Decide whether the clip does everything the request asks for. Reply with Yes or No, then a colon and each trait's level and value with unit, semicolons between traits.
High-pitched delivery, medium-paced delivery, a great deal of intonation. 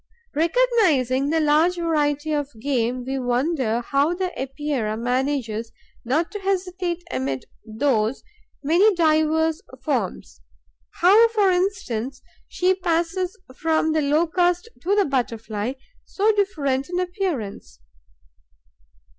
No: very high, 305 Hz; slow, 110 wpm; wide, 5.9 semitones